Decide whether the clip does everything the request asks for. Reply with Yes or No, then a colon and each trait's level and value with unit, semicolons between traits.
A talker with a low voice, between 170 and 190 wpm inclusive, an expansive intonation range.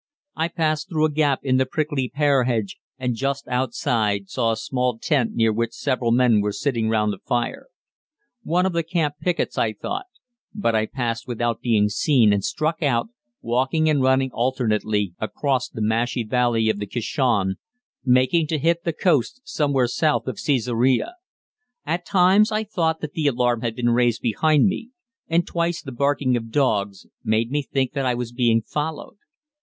No: low, 130 Hz; average, 180 wpm; average, 4.9 semitones